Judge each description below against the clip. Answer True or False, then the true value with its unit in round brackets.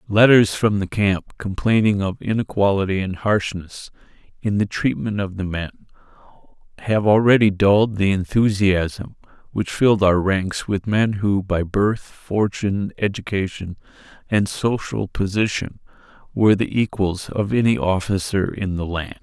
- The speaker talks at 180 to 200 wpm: False (135 wpm)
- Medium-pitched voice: False (100 Hz)